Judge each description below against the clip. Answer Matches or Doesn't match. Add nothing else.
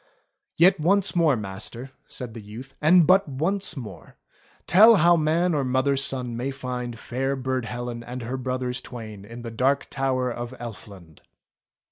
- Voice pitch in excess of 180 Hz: Doesn't match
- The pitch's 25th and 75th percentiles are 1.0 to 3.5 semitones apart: Doesn't match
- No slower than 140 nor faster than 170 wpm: Matches